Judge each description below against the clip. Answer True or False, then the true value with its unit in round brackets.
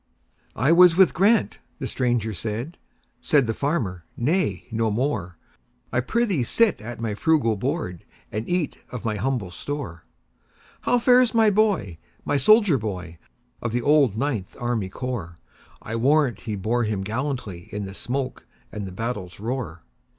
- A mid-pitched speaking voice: False (120 Hz)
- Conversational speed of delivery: False (130 wpm)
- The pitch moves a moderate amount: False (6.3 semitones)